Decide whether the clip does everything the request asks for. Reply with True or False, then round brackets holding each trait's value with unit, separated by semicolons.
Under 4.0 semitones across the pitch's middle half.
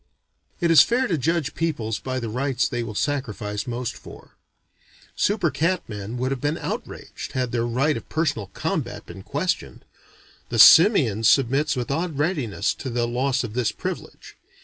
False (4.8 semitones)